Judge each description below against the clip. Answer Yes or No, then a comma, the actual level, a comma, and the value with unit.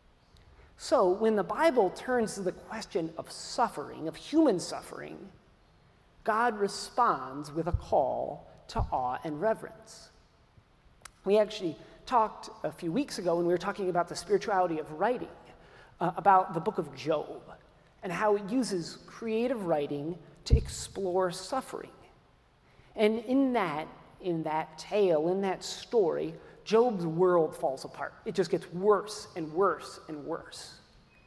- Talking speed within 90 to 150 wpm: Yes, average, 140 wpm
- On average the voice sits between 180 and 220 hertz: Yes, medium, 185 Hz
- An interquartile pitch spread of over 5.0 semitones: No, average, 4.7 semitones